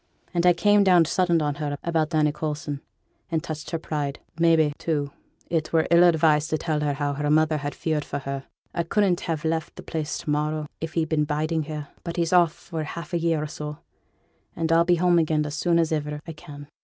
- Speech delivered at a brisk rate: Yes, fast, 225 wpm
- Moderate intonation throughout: No, narrow, 2.0 semitones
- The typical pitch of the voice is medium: Yes, medium, 155 Hz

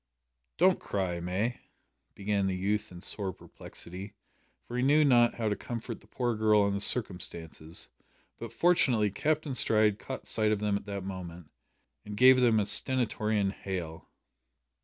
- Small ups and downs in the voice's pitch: No, average, 3.7 semitones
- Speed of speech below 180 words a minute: Yes, average, 160 wpm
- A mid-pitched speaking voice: No, low, 105 Hz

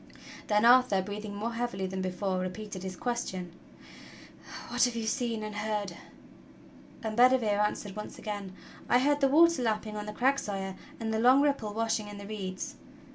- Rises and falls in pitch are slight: No, average, 3.1 semitones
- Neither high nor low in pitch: No, high, 215 Hz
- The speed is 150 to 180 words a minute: Yes, average, 175 wpm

